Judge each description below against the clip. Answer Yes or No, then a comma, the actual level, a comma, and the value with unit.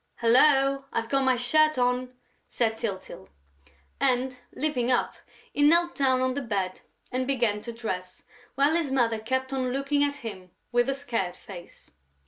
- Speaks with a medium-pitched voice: No, very high, 255 Hz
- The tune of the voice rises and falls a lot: No, average, 3.2 semitones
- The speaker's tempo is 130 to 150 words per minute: No, average, 160 wpm